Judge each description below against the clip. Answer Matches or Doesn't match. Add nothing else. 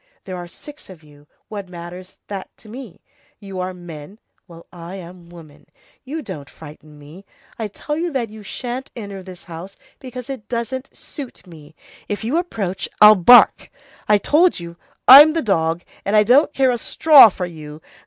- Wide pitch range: Matches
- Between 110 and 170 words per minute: Doesn't match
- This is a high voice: Matches